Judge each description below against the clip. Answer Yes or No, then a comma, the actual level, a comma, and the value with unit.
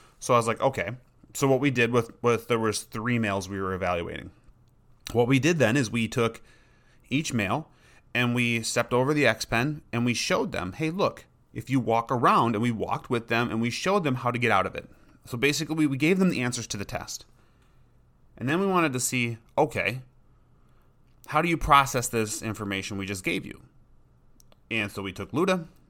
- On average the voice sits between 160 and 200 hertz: No, low, 120 Hz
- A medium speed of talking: No, fast, 215 wpm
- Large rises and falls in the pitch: No, narrow, 2.6 semitones